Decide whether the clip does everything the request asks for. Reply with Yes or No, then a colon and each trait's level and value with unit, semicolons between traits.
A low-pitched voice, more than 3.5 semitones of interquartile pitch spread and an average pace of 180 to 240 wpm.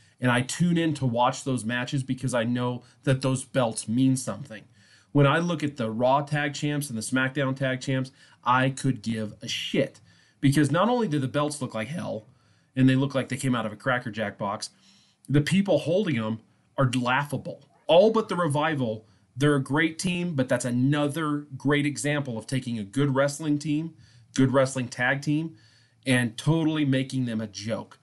No: low, 130 Hz; average, 3.2 semitones; average, 195 wpm